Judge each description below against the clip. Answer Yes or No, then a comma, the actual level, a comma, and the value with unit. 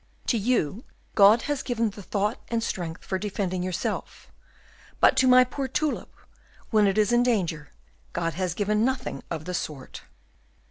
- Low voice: No, high, 210 Hz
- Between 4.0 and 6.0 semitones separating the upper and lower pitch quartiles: Yes, average, 4.9 semitones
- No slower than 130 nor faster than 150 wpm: No, average, 165 wpm